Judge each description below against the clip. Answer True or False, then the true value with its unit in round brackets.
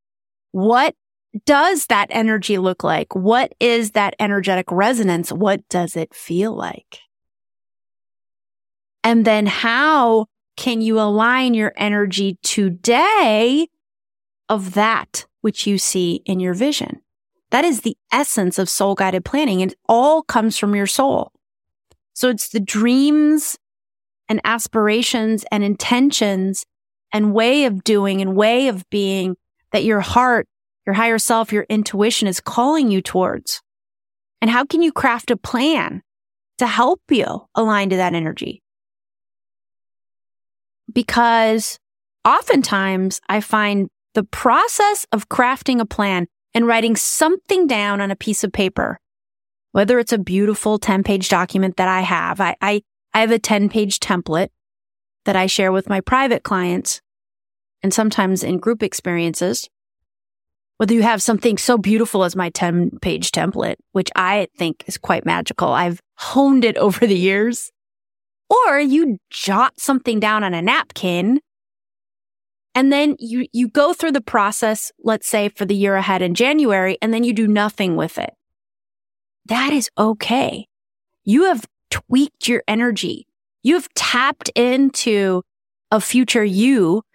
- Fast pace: False (140 wpm)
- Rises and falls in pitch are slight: False (4.3 semitones)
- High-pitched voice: True (210 Hz)